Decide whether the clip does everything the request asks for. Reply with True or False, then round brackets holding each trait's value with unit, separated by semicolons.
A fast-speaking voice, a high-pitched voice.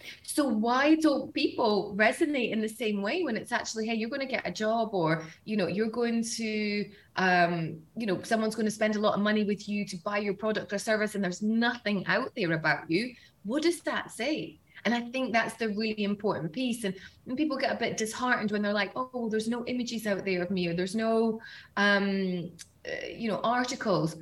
True (225 wpm; 215 Hz)